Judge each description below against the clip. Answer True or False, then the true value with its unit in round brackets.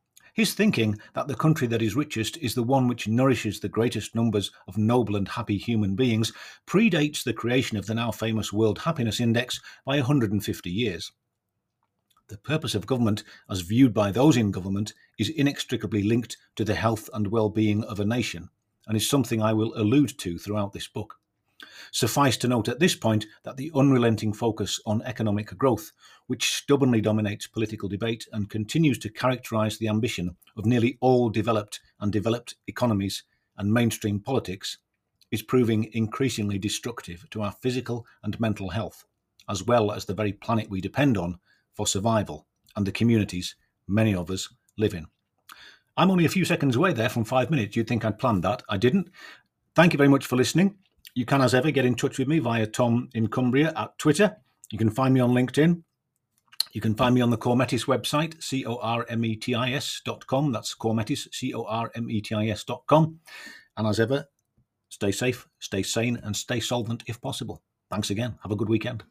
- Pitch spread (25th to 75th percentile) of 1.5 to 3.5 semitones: True (3.2 semitones)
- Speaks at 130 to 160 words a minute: False (195 wpm)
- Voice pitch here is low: True (115 Hz)